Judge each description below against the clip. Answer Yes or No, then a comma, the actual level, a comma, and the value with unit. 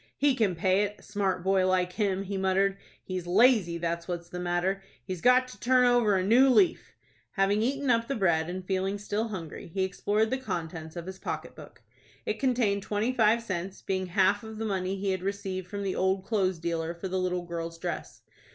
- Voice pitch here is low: No, high, 195 Hz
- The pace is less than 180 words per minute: No, fast, 205 wpm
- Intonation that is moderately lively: Yes, average, 3.0 semitones